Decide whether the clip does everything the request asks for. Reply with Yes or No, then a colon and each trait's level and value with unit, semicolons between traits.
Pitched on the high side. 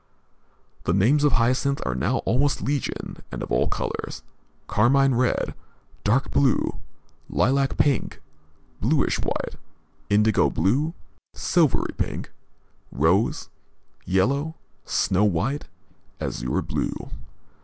No: low, 125 Hz